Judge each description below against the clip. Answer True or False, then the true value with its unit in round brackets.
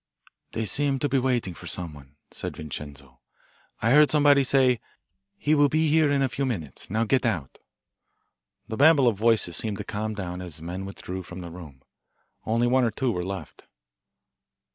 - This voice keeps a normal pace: True (180 wpm)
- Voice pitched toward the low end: True (110 Hz)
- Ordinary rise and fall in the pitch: False (7.2 semitones)